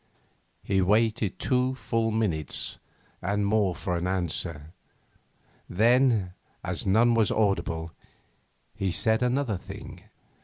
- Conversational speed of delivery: No, slow, 110 wpm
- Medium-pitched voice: No, low, 105 Hz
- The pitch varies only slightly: No, average, 4.1 semitones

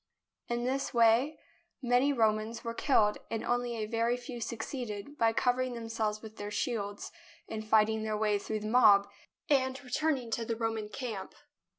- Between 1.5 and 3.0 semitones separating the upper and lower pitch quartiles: Yes, narrow, 2.4 semitones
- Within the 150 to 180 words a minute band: Yes, average, 165 wpm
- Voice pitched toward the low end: No, high, 230 Hz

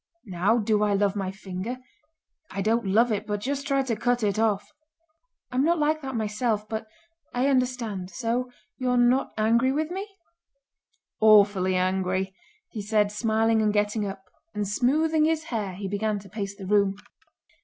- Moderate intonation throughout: Yes, average, 3.7 semitones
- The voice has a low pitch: No, high, 215 Hz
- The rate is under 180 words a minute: Yes, average, 165 wpm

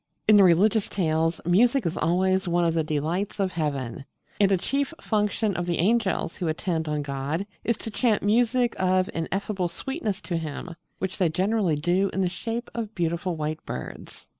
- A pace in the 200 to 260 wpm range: No, average, 185 wpm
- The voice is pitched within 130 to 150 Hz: No, medium, 185 Hz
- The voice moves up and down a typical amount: Yes, average, 4.2 semitones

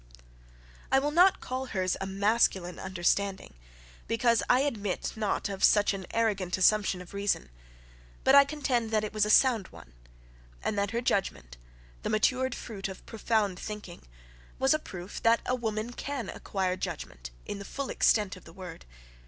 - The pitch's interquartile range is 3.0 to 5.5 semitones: Yes, average, 4.0 semitones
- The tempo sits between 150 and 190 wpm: Yes, average, 170 wpm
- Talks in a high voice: Yes, high, 210 Hz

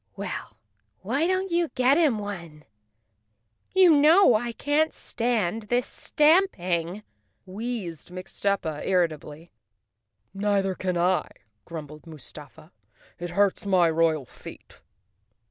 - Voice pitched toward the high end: Yes, high, 195 Hz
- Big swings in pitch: Yes, wide, 6.8 semitones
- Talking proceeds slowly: Yes, slow, 110 wpm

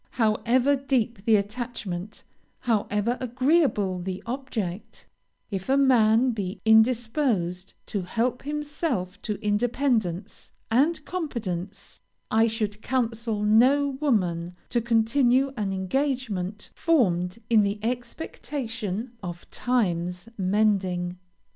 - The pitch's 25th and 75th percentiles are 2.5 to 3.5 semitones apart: No, average, 4.7 semitones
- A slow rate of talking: Yes, slow, 100 wpm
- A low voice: No, high, 225 Hz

